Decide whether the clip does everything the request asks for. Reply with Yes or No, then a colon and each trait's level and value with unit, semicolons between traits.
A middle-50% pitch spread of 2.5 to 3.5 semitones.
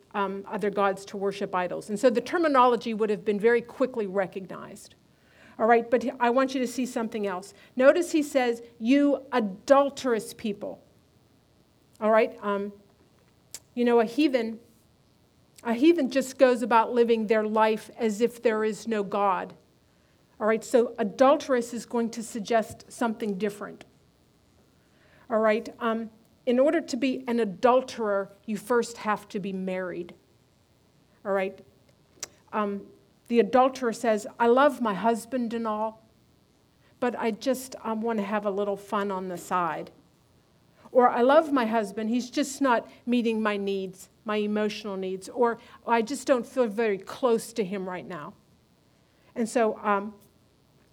Yes: average, 3.2 semitones